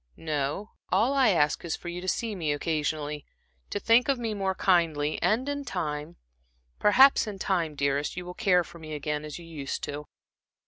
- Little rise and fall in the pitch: No, wide, 5.5 semitones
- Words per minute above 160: Yes, average, 190 wpm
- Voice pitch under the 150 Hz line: No, medium, 170 Hz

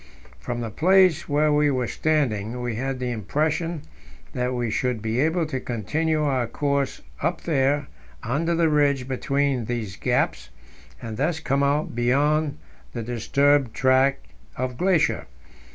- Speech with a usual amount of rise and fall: Yes, average, 3.8 semitones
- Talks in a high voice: No, medium, 140 Hz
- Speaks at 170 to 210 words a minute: No, average, 145 wpm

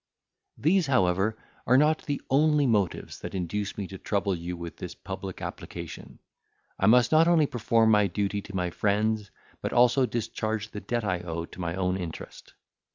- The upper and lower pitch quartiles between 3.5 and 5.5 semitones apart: Yes, average, 4.8 semitones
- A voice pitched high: No, low, 105 Hz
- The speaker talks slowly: No, average, 175 wpm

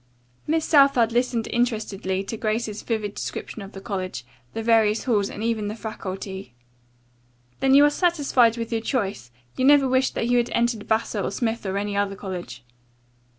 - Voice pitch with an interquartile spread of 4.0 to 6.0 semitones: No, average, 3.3 semitones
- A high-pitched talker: Yes, high, 225 Hz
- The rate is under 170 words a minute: No, average, 175 wpm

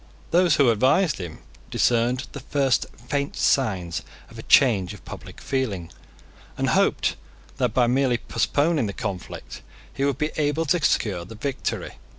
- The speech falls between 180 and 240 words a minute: No, average, 155 wpm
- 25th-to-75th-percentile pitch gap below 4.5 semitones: No, average, 5.3 semitones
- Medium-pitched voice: No, low, 130 Hz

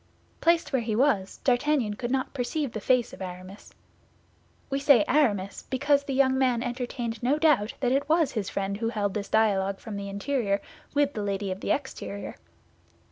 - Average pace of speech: Yes, average, 185 wpm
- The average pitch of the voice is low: No, high, 240 Hz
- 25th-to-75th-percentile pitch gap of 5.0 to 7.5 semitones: Yes, average, 5.3 semitones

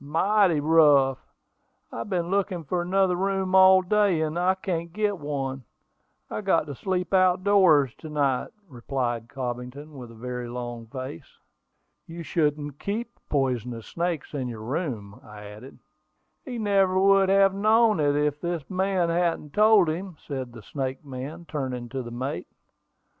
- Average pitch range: No, wide, 6.3 semitones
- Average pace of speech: Yes, average, 160 wpm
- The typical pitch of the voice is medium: Yes, medium, 155 Hz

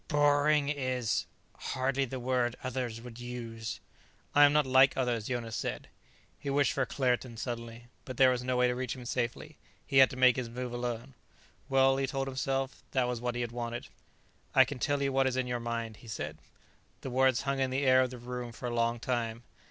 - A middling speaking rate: No, fast, 215 wpm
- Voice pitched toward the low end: Yes, low, 125 Hz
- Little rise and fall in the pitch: Yes, narrow, 2.0 semitones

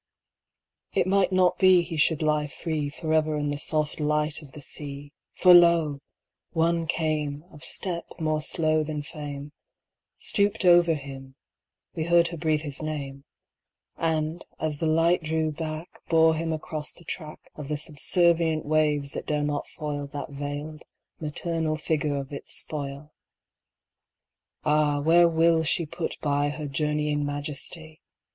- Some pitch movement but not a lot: No, narrow, 2.0 semitones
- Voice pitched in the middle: Yes, medium, 155 Hz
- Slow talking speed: Yes, slow, 125 wpm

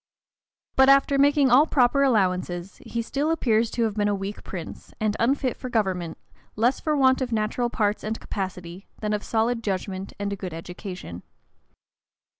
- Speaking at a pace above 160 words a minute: Yes, average, 170 wpm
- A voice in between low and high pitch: No, high, 215 Hz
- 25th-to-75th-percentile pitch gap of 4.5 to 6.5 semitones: Yes, average, 4.8 semitones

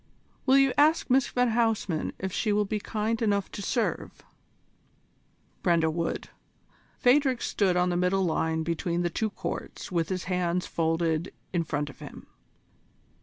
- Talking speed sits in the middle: Yes, average, 155 wpm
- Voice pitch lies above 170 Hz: Yes, medium, 185 Hz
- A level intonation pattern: No, average, 4.9 semitones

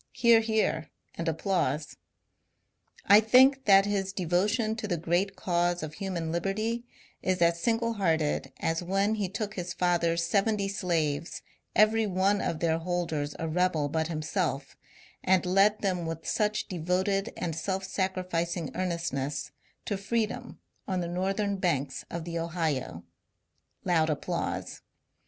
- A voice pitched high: No, medium, 180 Hz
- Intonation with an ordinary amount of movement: Yes, average, 3.3 semitones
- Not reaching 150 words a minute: Yes, average, 140 wpm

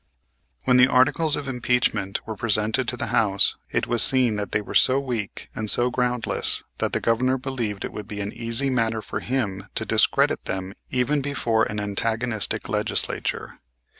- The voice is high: No, low, 115 Hz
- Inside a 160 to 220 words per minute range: Yes, average, 175 wpm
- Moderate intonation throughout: Yes, average, 3.3 semitones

